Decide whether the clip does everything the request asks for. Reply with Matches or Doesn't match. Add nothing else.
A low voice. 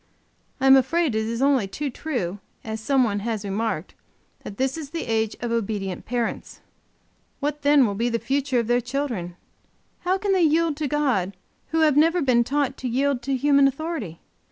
Doesn't match